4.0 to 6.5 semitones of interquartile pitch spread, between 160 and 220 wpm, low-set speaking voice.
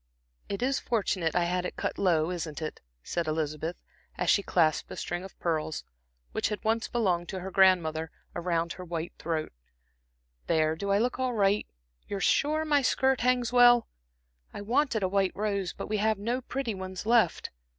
No: average, 5.2 semitones; average, 185 wpm; high, 195 Hz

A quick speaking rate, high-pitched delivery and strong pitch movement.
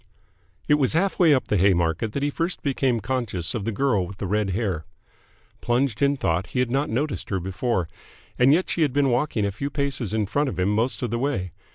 No: fast, 230 wpm; low, 120 Hz; wide, 5.8 semitones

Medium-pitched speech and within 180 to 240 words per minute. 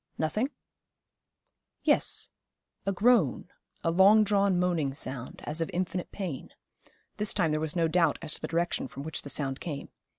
No: medium, 170 Hz; average, 165 wpm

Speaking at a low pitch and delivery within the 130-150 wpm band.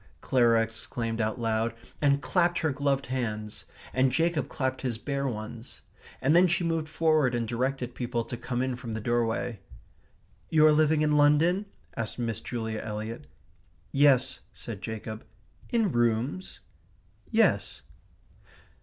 Yes: low, 125 Hz; average, 140 wpm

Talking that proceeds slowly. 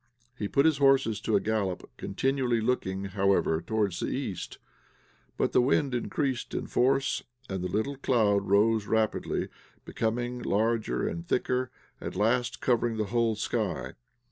No: average, 145 wpm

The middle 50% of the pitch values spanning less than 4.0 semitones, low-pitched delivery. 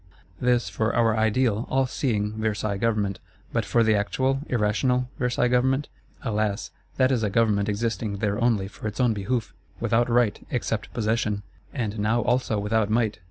Yes: average, 2.7 semitones; low, 110 Hz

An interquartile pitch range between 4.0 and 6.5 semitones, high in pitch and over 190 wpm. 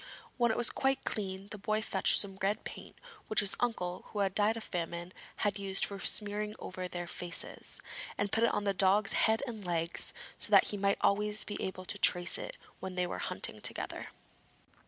No: narrow, 2.4 semitones; high, 200 Hz; average, 200 wpm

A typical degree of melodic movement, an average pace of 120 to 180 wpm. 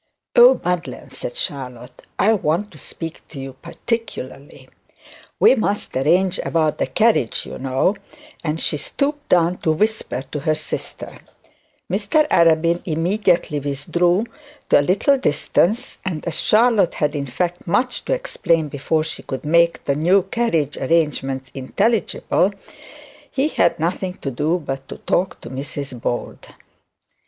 No: wide, 5.8 semitones; average, 140 wpm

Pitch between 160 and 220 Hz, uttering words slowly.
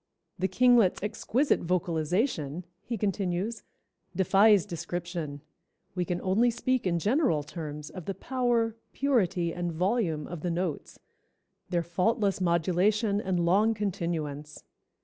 Yes: medium, 185 Hz; slow, 120 wpm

